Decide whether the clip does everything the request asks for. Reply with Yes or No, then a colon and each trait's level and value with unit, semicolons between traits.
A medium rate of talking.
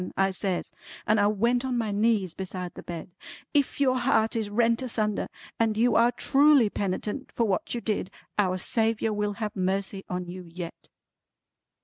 Yes: average, 170 wpm